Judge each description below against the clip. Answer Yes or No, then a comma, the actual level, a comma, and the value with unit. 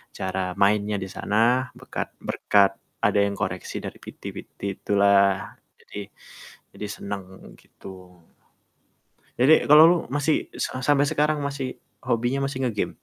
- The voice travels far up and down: Yes, wide, 5.7 semitones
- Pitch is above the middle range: No, low, 105 Hz